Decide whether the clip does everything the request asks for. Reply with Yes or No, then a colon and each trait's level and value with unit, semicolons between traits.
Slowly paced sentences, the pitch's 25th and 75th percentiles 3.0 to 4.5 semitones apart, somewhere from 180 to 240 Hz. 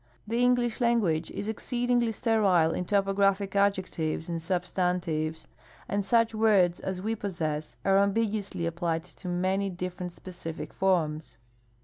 Yes: slow, 125 wpm; average, 3.6 semitones; high, 190 Hz